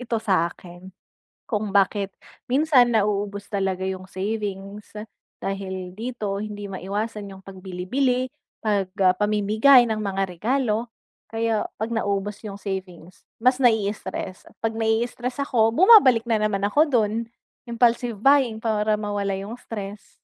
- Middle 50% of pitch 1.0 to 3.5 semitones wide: Yes, average, 2.8 semitones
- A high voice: Yes, high, 210 Hz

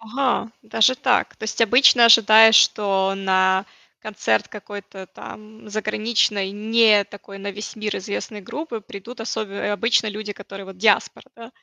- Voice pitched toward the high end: Yes, high, 215 Hz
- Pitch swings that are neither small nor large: No, narrow, 2.1 semitones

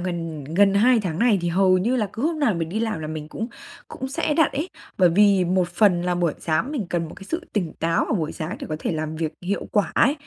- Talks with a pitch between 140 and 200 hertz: Yes, medium, 185 Hz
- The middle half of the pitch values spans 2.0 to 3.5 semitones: No, average, 5.0 semitones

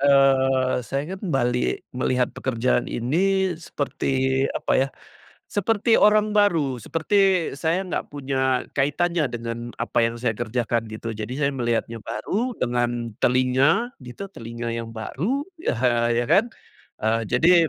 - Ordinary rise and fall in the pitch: No, wide, 5.8 semitones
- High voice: No, low, 130 Hz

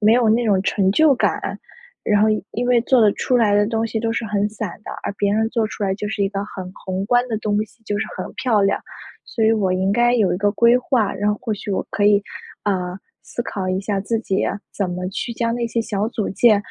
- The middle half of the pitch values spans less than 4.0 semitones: Yes, narrow, 2.6 semitones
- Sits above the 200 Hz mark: Yes, high, 210 Hz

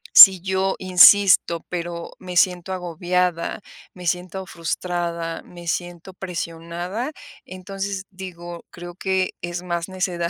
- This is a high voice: No, medium, 180 Hz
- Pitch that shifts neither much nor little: No, narrow, 1.6 semitones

